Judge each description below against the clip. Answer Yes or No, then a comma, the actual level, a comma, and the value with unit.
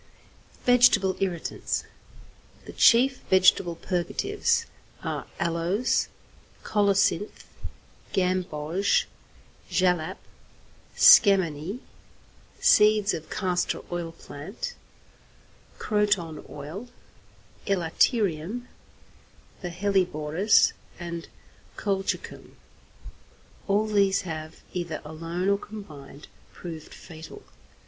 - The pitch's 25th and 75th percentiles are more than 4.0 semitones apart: No, average, 3.5 semitones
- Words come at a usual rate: No, slow, 75 wpm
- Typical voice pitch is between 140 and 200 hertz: Yes, medium, 185 Hz